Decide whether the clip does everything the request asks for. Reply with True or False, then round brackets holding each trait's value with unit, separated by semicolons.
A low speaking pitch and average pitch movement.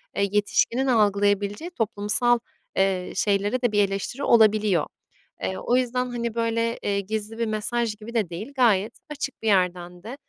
False (215 Hz; 3.0 semitones)